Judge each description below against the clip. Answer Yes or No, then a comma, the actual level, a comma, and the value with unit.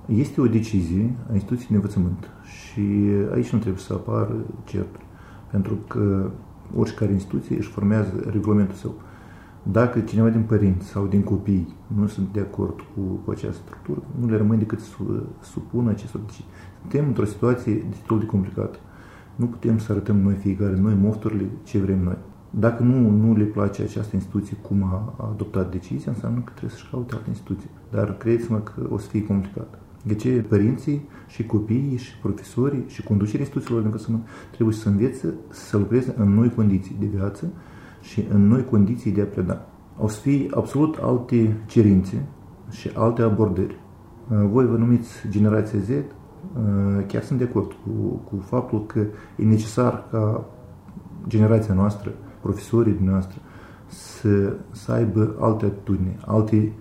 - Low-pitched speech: Yes, low, 105 Hz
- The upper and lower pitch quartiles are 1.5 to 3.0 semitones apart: Yes, narrow, 2.4 semitones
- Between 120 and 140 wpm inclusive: No, average, 160 wpm